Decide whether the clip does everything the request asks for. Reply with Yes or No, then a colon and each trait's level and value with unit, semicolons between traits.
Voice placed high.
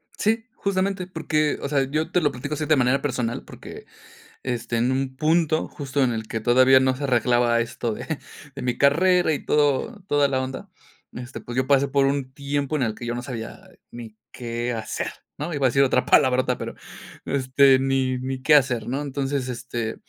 No: low, 135 Hz